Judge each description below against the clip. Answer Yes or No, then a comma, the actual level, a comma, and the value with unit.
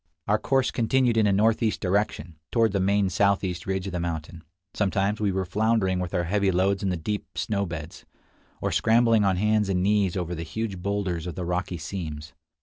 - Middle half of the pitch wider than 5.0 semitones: No, average, 3.0 semitones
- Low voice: Yes, very low, 95 Hz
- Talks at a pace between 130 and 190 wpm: No, average, 200 wpm